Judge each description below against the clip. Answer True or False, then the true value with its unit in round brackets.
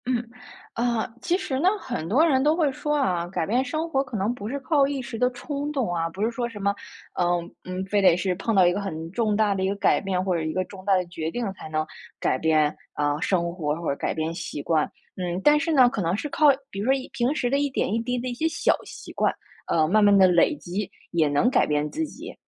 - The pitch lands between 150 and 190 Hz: False (205 Hz)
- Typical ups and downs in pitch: False (6.7 semitones)